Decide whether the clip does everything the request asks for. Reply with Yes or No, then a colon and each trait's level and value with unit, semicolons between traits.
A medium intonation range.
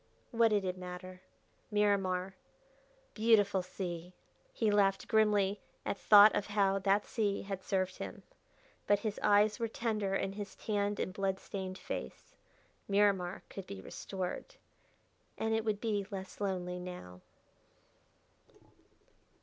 No: narrow, 1.9 semitones